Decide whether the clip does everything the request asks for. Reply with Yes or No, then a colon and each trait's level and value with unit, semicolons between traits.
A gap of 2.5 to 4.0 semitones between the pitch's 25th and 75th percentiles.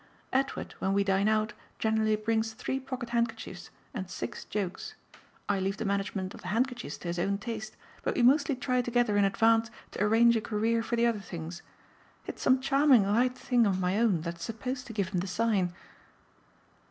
Yes: average, 3.4 semitones